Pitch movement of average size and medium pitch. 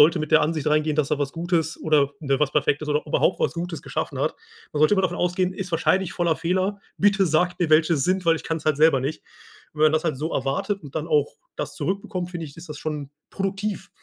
Yes: average, 3.1 semitones; medium, 160 Hz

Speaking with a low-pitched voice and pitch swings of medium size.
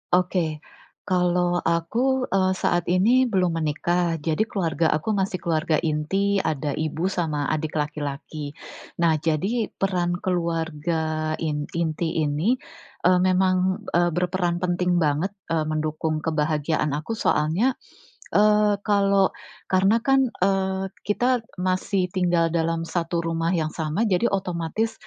No: medium, 175 Hz; average, 3.3 semitones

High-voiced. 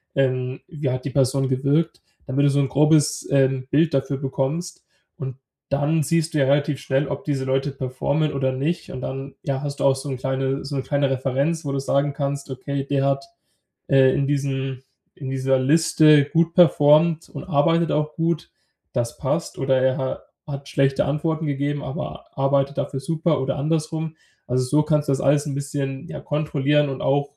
No: medium, 140 Hz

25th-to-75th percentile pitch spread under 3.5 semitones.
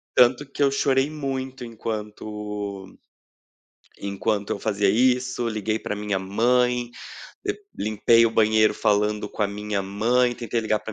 Yes: average, 2.9 semitones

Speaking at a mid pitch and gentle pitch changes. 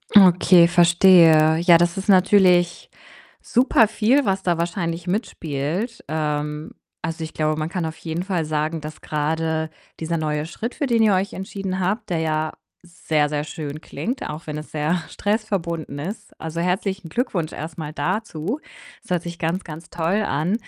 No: medium, 170 Hz; average, 3.5 semitones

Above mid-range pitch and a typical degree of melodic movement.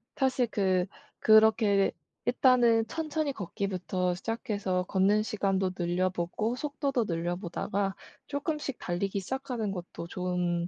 Yes: high, 200 Hz; average, 5.0 semitones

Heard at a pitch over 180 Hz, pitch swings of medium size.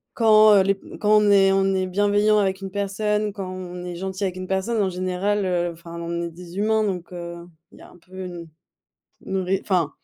No: high, 190 Hz; narrow, 2.3 semitones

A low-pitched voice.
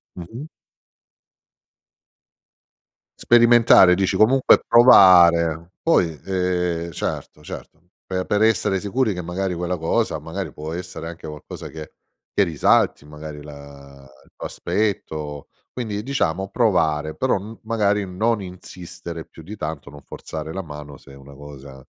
Yes: very low, 90 Hz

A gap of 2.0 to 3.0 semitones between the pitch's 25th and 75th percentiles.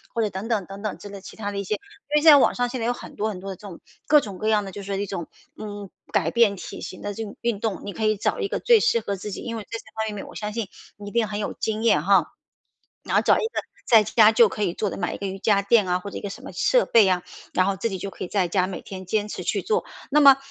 Yes: average, 2.7 semitones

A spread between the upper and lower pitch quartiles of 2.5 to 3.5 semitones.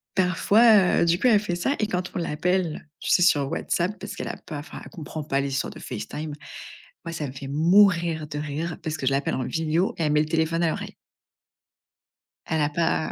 Yes: average, 3.1 semitones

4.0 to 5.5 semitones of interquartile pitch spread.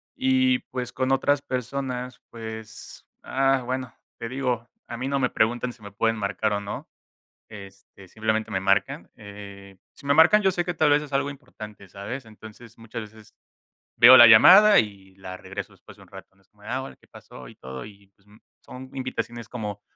Yes: average, 4.5 semitones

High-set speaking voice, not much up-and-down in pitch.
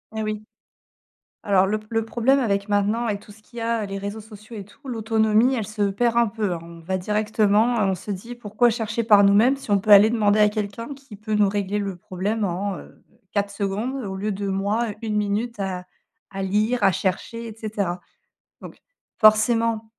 Yes: high, 210 Hz; narrow, 2.1 semitones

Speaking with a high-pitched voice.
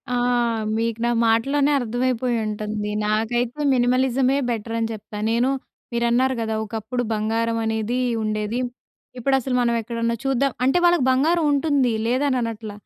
Yes: high, 235 Hz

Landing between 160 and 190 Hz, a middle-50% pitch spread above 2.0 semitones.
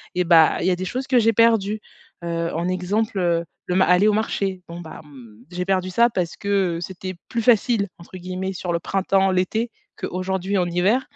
Yes: medium, 185 Hz; average, 2.7 semitones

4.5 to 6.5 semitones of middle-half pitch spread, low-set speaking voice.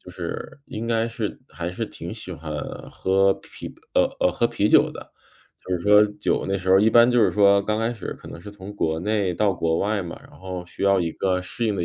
No: average, 2.9 semitones; low, 100 Hz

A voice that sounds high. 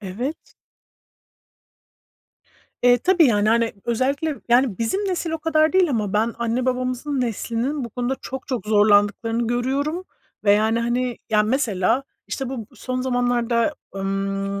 Yes: high, 240 Hz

